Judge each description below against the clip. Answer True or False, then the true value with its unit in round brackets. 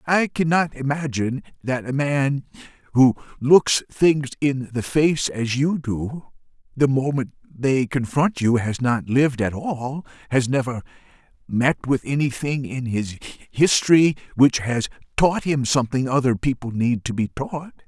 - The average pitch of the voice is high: False (135 Hz)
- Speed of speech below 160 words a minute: True (150 wpm)